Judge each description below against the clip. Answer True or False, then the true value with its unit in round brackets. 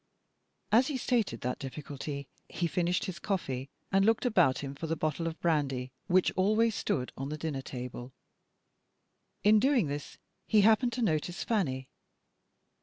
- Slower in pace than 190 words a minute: True (155 wpm)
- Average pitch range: False (7.4 semitones)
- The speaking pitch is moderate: True (165 Hz)